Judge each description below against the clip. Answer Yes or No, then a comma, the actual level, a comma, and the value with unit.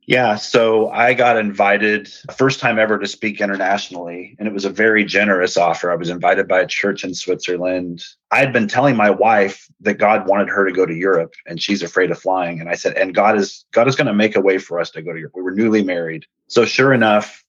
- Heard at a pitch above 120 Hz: No, low, 100 Hz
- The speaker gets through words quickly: Yes, fast, 240 wpm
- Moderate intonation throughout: Yes, average, 3.0 semitones